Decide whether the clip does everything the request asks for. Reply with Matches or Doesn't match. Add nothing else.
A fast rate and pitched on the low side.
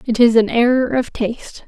Doesn't match